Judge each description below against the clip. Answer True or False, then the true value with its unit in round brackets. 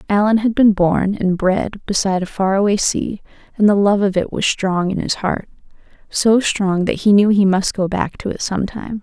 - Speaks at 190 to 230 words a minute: True (205 wpm)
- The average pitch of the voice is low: False (200 Hz)